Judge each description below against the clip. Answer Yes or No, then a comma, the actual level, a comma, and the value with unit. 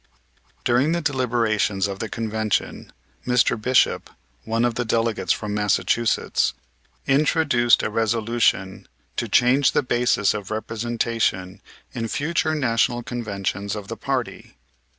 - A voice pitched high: No, low, 115 Hz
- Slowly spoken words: Yes, slow, 120 wpm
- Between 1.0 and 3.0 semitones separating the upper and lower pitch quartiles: Yes, narrow, 2.6 semitones